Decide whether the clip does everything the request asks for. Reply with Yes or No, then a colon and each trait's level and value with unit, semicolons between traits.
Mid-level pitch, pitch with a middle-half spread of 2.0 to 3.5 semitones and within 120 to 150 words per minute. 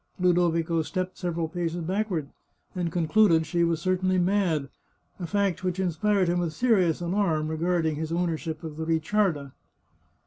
Yes: medium, 175 Hz; narrow, 2.4 semitones; average, 145 wpm